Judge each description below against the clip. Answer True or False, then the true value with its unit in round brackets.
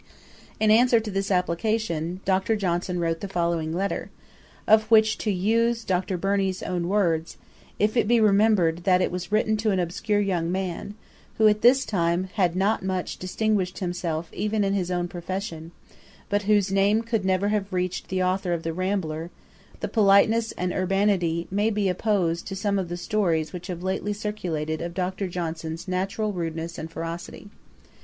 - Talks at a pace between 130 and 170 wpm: False (180 wpm)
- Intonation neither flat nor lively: True (3.1 semitones)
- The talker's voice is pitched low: False (190 Hz)